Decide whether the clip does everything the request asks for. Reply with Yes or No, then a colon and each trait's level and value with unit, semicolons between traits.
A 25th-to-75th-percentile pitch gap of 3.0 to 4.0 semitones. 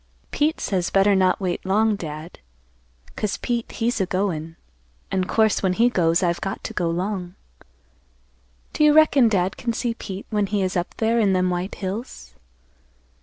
Yes: average, 3.5 semitones